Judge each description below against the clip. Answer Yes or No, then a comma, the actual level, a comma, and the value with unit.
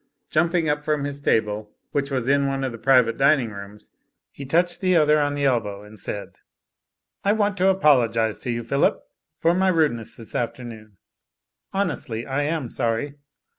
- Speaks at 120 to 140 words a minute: No, average, 170 wpm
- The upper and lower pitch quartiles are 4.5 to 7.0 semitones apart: Yes, average, 5.0 semitones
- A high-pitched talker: No, low, 135 Hz